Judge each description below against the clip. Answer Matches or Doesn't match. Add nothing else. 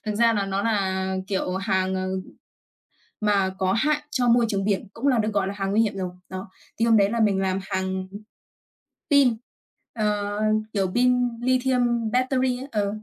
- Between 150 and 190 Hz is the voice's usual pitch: Doesn't match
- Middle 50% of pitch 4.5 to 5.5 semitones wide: Doesn't match